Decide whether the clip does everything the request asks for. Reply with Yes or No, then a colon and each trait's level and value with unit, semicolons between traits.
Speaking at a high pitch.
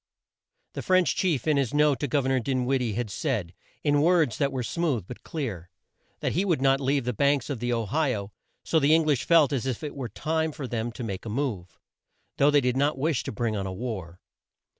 No: low, 135 Hz